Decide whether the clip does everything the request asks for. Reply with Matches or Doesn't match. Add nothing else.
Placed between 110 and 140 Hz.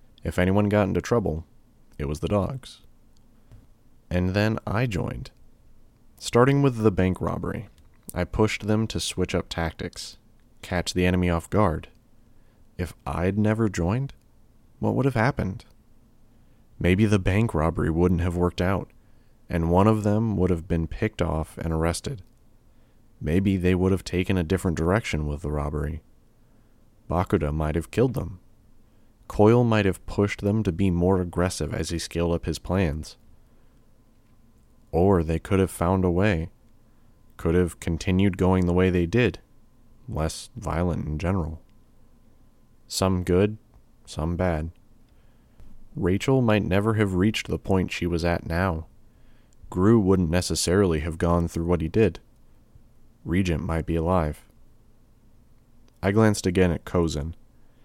Doesn't match